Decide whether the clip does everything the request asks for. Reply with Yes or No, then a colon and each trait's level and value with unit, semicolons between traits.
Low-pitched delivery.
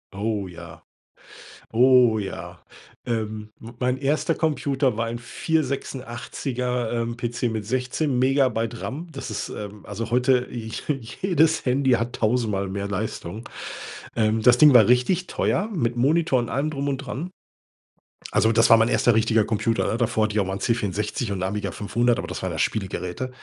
Yes: low, 120 Hz